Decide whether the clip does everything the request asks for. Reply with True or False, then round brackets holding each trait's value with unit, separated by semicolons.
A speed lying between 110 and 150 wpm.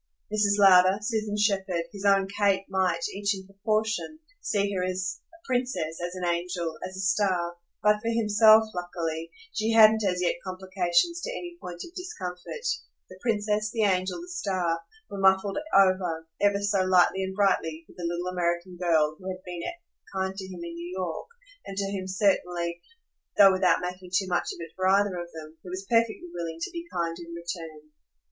False (185 wpm)